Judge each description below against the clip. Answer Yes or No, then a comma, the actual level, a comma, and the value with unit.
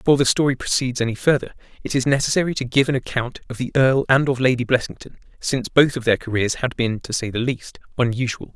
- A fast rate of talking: Yes, fast, 225 wpm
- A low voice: Yes, low, 125 Hz